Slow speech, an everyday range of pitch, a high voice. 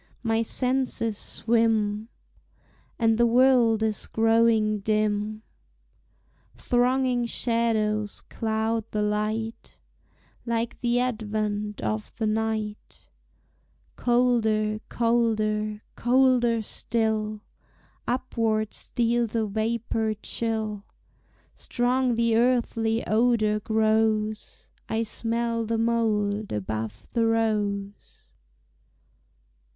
No: slow, 85 wpm; narrow, 1.6 semitones; high, 225 Hz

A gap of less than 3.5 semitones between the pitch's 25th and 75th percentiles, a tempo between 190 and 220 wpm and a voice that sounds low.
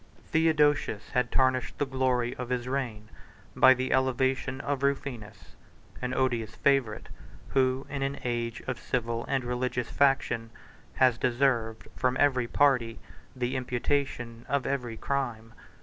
No: narrow, 2.4 semitones; slow, 135 wpm; low, 130 Hz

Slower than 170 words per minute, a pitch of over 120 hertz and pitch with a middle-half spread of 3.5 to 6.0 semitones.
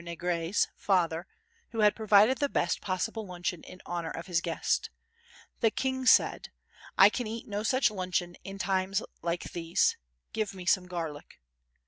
Yes: average, 150 wpm; medium, 185 Hz; average, 3.8 semitones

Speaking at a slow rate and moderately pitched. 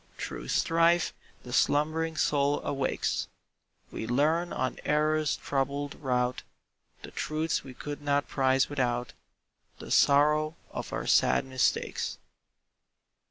Yes: slow, 115 wpm; medium, 145 Hz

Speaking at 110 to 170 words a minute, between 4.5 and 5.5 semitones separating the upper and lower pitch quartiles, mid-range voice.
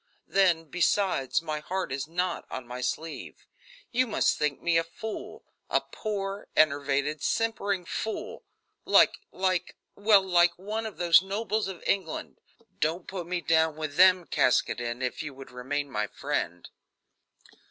Yes: average, 145 wpm; average, 5.0 semitones; medium, 170 Hz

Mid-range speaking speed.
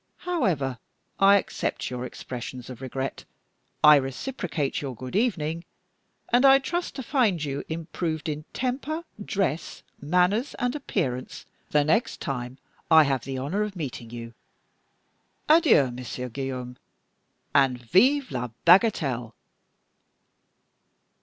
No: slow, 120 wpm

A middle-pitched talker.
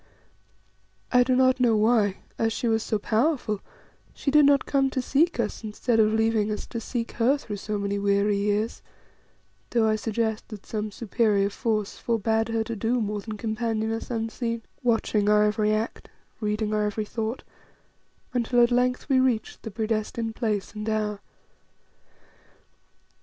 No: high, 220 Hz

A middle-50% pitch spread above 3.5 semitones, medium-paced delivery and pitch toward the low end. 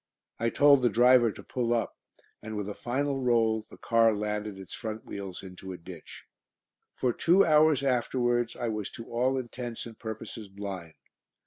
No: average, 3.1 semitones; average, 175 wpm; low, 115 Hz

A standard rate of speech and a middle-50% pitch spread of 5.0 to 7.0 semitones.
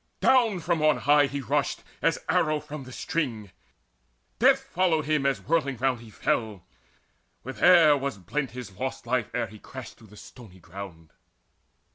Yes: average, 165 wpm; wide, 5.6 semitones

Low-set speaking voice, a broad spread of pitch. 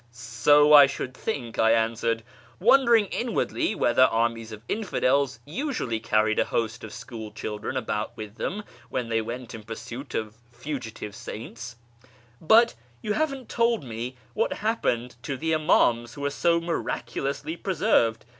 Yes: low, 125 Hz; wide, 6.8 semitones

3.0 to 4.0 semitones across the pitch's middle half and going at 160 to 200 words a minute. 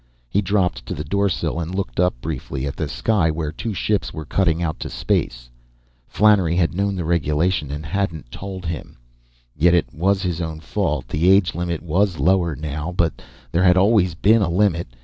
Yes: average, 3.7 semitones; average, 190 wpm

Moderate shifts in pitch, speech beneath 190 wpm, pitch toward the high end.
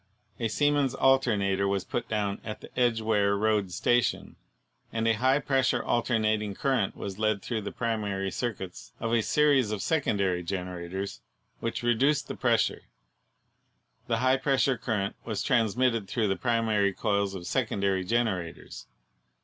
No: average, 3.6 semitones; average, 150 wpm; low, 110 Hz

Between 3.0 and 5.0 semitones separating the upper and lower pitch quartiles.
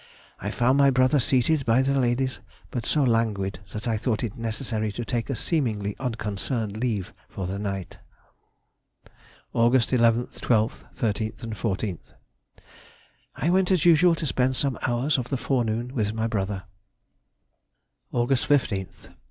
Yes: average, 3.5 semitones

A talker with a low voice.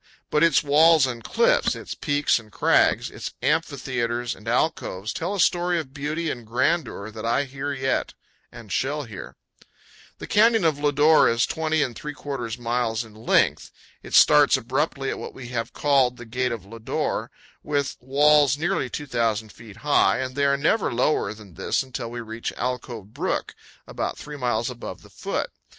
Yes: low, 130 Hz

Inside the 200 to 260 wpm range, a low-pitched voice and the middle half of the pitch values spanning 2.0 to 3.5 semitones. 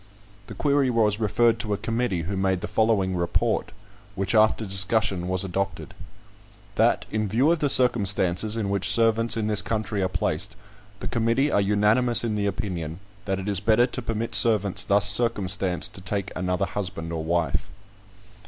No: average, 170 wpm; low, 100 Hz; average, 3.2 semitones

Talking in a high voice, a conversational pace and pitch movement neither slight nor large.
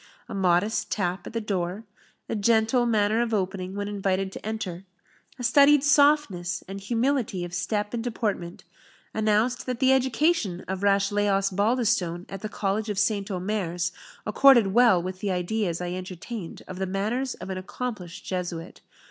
Yes: high, 205 Hz; average, 160 wpm; average, 3.7 semitones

